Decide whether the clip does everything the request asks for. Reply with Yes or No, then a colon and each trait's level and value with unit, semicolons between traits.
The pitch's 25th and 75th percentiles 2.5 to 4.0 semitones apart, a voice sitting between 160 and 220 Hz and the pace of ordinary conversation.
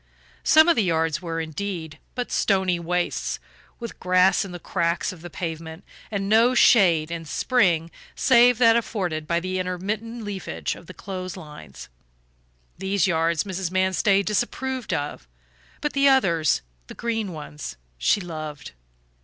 No: average, 4.4 semitones; medium, 185 Hz; average, 145 wpm